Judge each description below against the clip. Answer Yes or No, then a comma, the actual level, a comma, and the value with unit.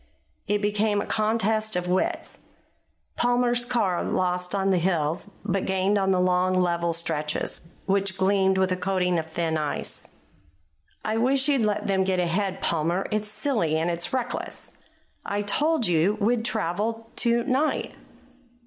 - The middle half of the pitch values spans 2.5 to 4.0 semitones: Yes, average, 3.4 semitones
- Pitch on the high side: Yes, high, 195 Hz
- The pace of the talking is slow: No, average, 150 wpm